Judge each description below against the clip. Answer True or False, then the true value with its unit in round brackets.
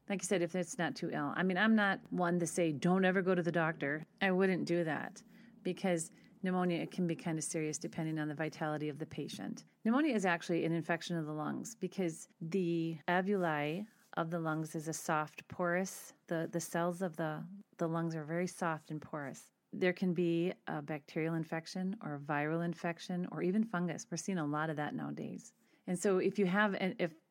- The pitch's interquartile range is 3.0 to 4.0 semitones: False (2.6 semitones)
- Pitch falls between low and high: True (175 Hz)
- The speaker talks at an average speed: False (210 wpm)